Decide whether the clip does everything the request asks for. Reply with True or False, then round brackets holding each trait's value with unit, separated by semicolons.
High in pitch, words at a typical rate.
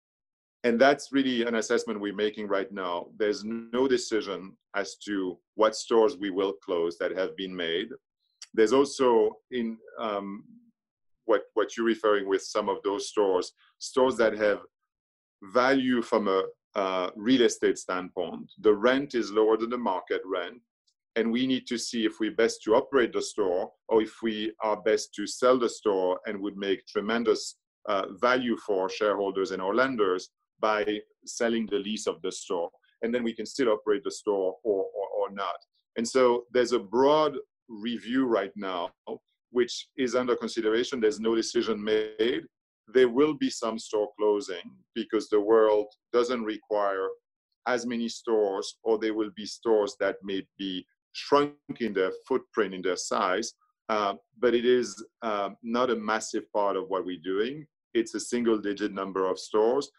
False (120 Hz; 170 wpm)